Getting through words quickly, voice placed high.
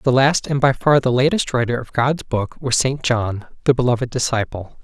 No: fast, 210 wpm; low, 125 Hz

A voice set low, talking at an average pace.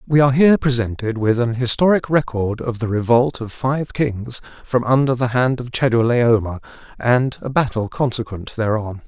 Yes: low, 125 Hz; average, 165 wpm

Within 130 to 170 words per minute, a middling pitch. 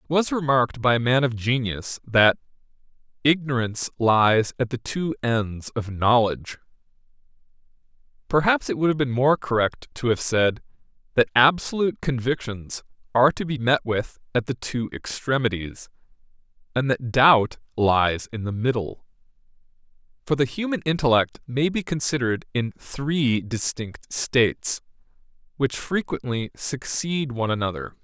No: slow, 135 wpm; low, 125 Hz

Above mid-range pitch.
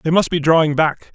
No: medium, 160 Hz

